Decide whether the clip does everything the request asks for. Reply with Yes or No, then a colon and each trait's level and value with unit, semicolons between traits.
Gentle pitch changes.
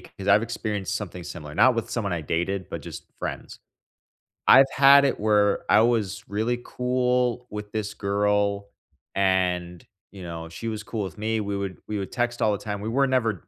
No: average, 3.2 semitones